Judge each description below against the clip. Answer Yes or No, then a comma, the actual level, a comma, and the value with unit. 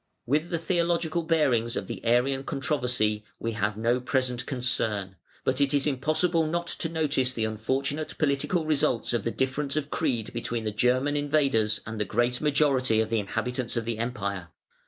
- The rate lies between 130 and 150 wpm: No, average, 175 wpm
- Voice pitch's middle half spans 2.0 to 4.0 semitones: No, average, 4.6 semitones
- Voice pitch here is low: Yes, low, 130 Hz